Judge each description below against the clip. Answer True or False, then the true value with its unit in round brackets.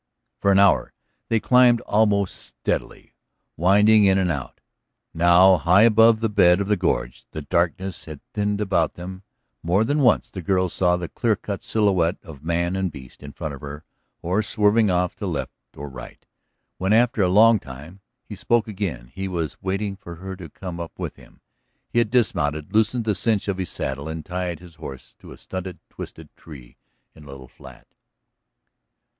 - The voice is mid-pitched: False (95 Hz)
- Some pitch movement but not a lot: True (4.1 semitones)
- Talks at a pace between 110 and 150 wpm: False (185 wpm)